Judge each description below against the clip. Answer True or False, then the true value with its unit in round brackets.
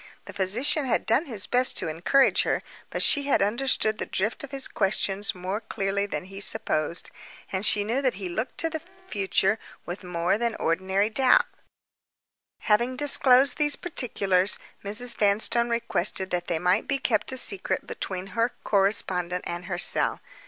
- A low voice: False (210 Hz)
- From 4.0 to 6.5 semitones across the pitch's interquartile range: True (4.8 semitones)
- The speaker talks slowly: False (165 wpm)